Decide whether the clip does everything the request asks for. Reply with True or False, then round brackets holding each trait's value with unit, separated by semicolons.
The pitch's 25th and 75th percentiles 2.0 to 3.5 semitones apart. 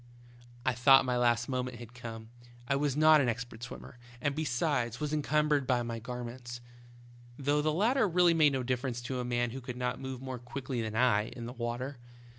True (2.6 semitones)